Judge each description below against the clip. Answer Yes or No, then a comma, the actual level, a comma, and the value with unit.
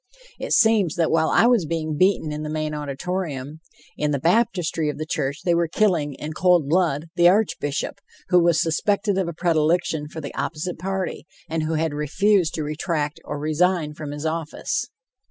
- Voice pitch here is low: No, medium, 160 Hz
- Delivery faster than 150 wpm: Yes, average, 185 wpm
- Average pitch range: Yes, average, 3.0 semitones